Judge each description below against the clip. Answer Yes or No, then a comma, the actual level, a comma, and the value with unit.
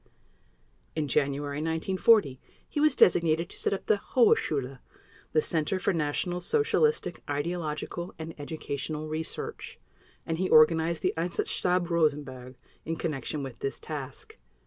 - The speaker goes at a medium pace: No, slow, 130 wpm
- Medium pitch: Yes, medium, 160 Hz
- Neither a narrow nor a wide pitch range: Yes, average, 3.3 semitones